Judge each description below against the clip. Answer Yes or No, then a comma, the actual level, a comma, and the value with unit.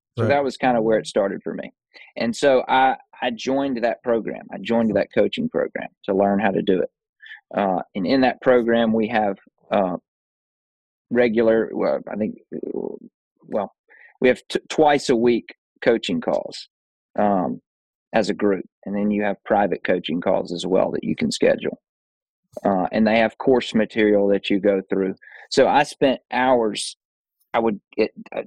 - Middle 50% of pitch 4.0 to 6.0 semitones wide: No, average, 3.5 semitones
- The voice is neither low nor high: No, low, 115 Hz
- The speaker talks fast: No, average, 175 wpm